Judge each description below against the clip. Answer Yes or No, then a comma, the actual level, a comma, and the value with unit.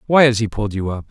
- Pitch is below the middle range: Yes, low, 110 Hz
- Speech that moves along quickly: Yes, fast, 325 wpm